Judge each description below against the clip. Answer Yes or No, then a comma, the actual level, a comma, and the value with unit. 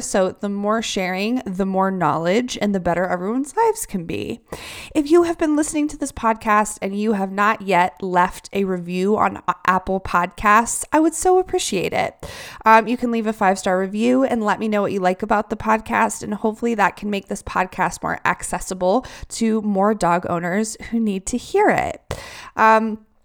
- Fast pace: No, average, 195 wpm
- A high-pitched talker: Yes, high, 215 Hz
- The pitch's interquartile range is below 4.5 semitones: Yes, average, 3.5 semitones